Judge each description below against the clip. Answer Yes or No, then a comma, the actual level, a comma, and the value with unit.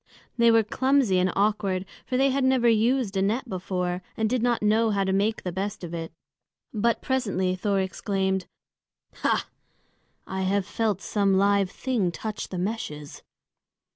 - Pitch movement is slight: No, average, 3.4 semitones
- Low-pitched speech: No, high, 200 Hz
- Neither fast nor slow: Yes, average, 160 wpm